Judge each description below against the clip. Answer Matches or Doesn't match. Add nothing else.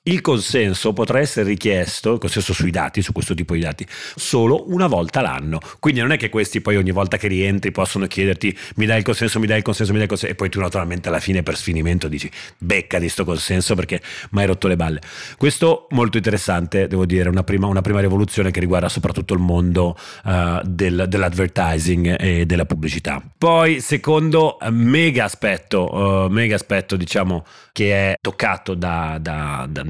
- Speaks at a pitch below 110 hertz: Matches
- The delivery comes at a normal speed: Doesn't match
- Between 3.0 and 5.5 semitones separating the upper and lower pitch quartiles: Matches